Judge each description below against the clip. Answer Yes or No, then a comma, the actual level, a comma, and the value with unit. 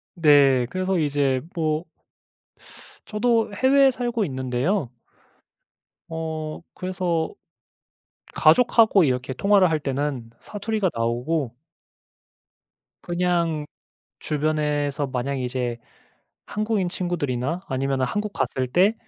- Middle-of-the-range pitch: Yes, medium, 155 Hz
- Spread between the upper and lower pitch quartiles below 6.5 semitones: Yes, wide, 6.0 semitones